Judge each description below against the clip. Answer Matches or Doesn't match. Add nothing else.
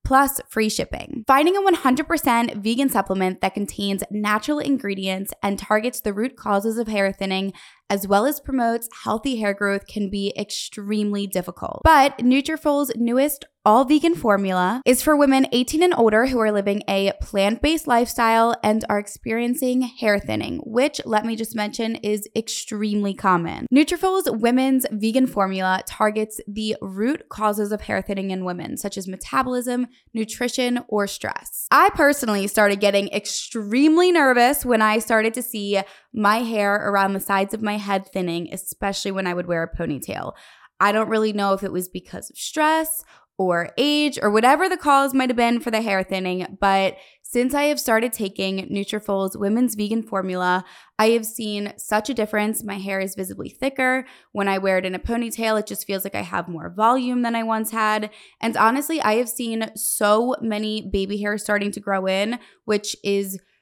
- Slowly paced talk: Doesn't match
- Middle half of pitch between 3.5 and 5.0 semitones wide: Matches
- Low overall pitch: Doesn't match